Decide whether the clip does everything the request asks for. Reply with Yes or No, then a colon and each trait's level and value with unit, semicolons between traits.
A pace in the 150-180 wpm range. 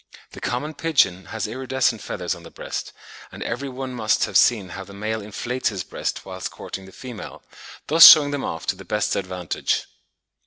No: average, 190 wpm